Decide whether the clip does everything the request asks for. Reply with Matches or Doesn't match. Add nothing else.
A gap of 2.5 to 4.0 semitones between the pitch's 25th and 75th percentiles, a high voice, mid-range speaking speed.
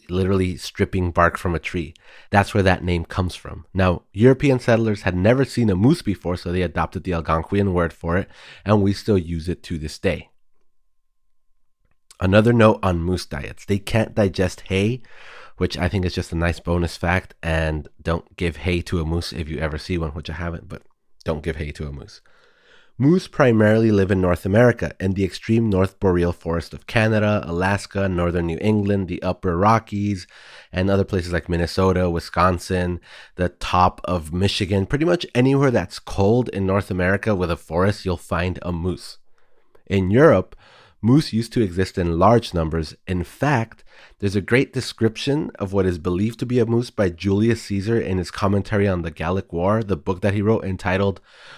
Doesn't match